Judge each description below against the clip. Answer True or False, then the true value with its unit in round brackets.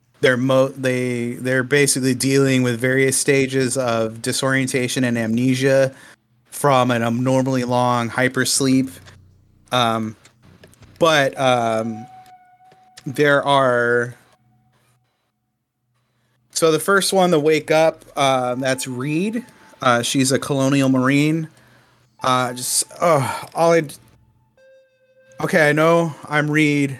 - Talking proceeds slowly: True (105 wpm)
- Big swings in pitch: False (2.9 semitones)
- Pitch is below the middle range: True (130 Hz)